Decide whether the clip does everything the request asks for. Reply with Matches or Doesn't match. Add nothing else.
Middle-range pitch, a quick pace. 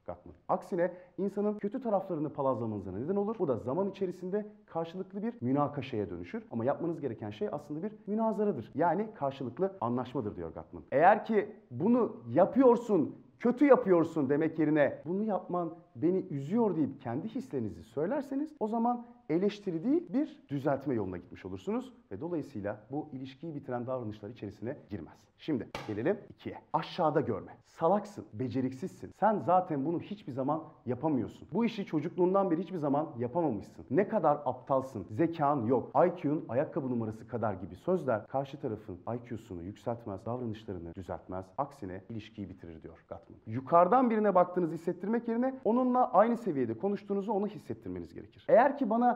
Matches